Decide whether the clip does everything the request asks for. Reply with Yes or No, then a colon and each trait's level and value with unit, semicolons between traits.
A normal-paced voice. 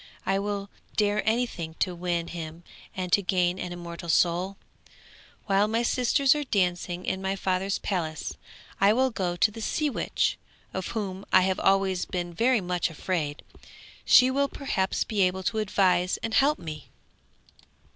Yes: average, 160 wpm